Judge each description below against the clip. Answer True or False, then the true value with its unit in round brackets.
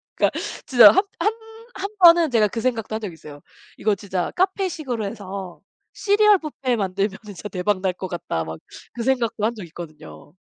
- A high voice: True (215 Hz)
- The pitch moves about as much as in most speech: False (6.1 semitones)